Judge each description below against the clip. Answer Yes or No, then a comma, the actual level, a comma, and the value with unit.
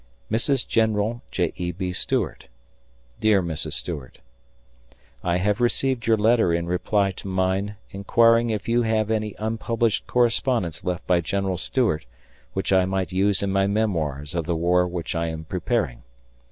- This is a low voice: Yes, very low, 95 Hz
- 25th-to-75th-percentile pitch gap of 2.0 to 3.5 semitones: No, average, 4.0 semitones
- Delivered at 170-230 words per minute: No, average, 155 wpm